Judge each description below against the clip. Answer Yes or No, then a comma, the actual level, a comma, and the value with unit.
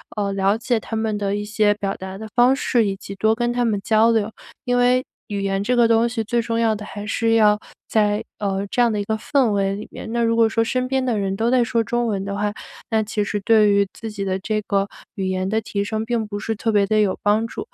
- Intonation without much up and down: Yes, narrow, 2.3 semitones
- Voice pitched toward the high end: Yes, high, 215 Hz